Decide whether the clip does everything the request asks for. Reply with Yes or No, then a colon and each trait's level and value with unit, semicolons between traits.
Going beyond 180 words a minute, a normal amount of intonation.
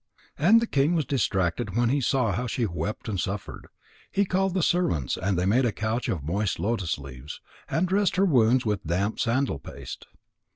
No: average, 195 wpm; wide, 7.1 semitones